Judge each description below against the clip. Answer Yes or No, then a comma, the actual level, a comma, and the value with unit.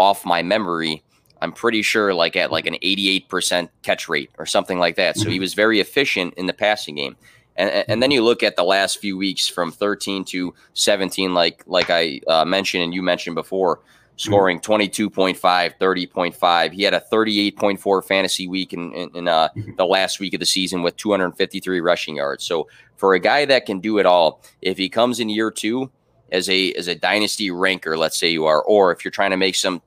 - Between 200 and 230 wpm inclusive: Yes, fast, 205 wpm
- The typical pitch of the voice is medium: No, very low, 95 Hz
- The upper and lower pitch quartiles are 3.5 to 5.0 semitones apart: No, narrow, 2.4 semitones